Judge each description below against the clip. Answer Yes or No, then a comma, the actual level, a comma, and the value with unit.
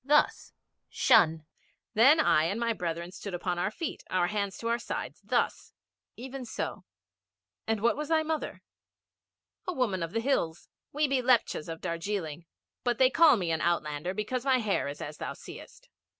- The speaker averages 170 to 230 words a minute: Yes, average, 175 wpm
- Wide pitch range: Yes, wide, 7.1 semitones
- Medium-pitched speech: No, high, 215 Hz